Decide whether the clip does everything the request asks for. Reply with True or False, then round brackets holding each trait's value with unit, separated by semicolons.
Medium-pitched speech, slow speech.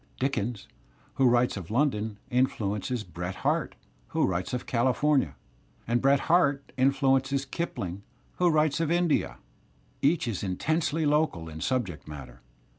False (125 Hz; 130 wpm)